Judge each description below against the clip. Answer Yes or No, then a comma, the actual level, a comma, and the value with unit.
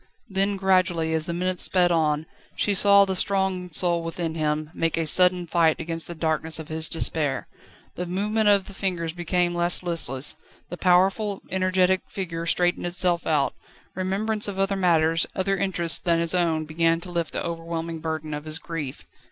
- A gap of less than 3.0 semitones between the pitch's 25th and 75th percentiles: Yes, narrow, 2.5 semitones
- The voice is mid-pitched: Yes, medium, 175 Hz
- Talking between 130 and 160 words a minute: No, average, 175 wpm